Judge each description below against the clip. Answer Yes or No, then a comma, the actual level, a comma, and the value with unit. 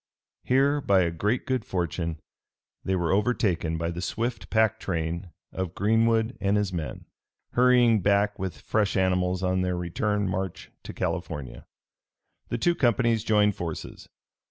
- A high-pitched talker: No, low, 100 Hz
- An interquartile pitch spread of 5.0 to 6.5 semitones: No, average, 4.0 semitones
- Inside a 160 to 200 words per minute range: No, average, 140 wpm